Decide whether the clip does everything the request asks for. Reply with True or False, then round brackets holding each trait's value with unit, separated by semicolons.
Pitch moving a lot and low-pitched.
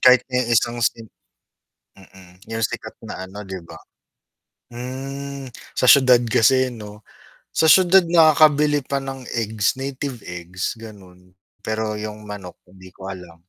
True (5.8 semitones; 115 Hz)